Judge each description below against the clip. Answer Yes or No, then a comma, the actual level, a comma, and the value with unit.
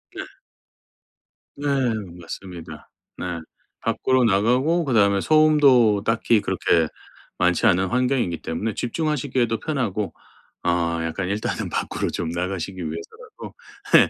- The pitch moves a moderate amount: No, wide, 5.9 semitones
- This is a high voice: No, low, 105 Hz